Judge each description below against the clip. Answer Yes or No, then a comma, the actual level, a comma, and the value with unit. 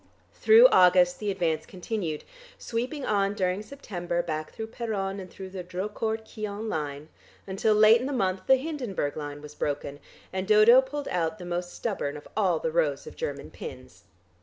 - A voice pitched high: Yes, high, 195 Hz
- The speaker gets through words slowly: No, average, 175 wpm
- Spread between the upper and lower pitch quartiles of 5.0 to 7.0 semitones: No, average, 4.4 semitones